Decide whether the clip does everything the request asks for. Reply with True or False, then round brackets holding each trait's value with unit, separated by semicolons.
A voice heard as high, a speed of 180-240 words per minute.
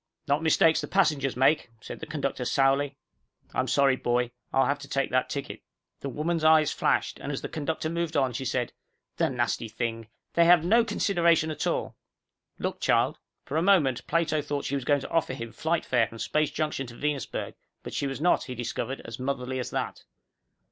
False (140 Hz; 200 wpm)